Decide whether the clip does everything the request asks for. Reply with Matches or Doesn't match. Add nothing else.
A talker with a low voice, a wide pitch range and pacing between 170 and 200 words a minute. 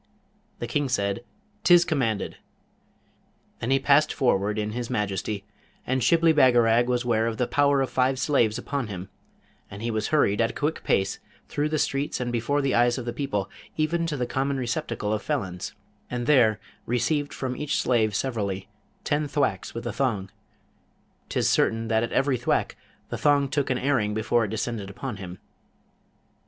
Doesn't match